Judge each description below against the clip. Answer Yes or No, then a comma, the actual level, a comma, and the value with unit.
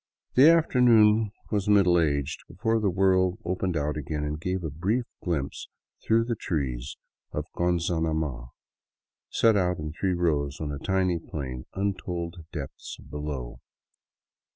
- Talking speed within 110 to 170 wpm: Yes, average, 140 wpm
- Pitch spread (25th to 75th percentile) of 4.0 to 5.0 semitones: Yes, average, 4.7 semitones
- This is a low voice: Yes, very low, 85 Hz